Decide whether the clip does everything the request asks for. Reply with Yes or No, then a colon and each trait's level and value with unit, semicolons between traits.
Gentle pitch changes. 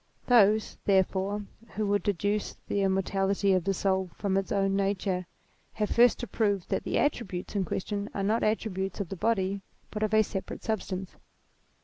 Yes: narrow, 1.8 semitones